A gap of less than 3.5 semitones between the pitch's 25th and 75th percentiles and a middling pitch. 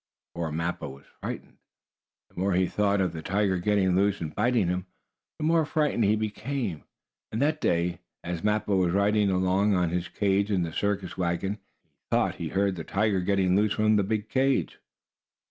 No: average, 2.9 semitones; low, 100 Hz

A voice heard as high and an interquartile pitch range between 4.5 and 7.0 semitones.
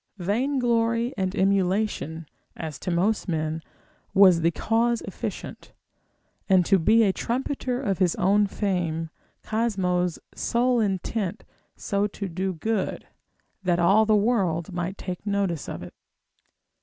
No: high, 195 Hz; average, 3.9 semitones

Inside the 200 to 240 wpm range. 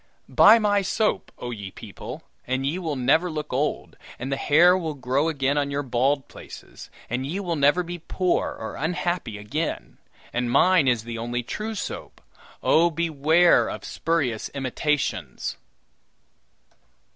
No: average, 150 wpm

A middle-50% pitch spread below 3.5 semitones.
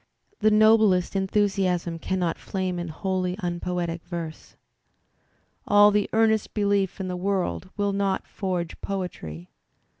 Yes: narrow, 2.4 semitones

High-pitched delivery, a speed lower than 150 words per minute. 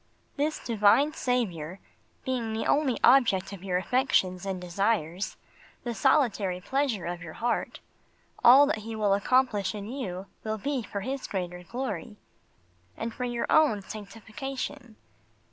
Yes: high, 220 Hz; average, 140 wpm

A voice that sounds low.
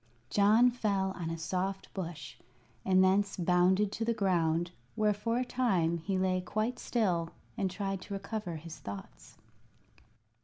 No: high, 190 Hz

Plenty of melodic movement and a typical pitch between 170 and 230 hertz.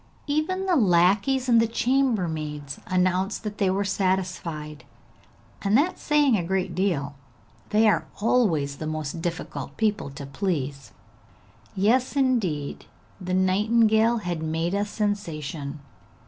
Yes: wide, 5.8 semitones; high, 190 Hz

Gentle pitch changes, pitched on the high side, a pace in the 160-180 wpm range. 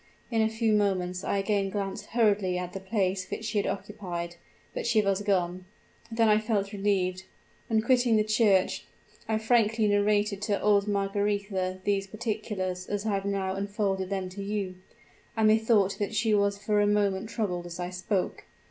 Yes: narrow, 2.0 semitones; high, 200 Hz; average, 175 wpm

